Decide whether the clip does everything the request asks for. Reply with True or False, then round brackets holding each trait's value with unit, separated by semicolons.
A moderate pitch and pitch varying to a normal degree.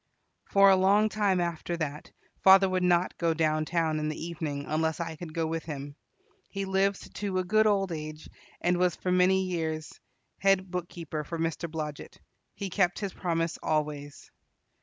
True (170 Hz; 3.3 semitones)